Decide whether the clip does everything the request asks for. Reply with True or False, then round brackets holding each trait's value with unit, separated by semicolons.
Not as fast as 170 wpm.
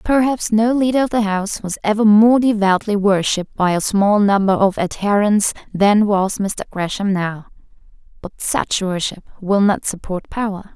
True (160 wpm)